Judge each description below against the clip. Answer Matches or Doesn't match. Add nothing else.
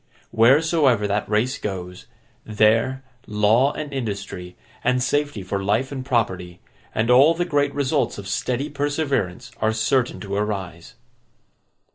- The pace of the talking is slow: Matches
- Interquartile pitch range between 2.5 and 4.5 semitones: Doesn't match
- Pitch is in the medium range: Doesn't match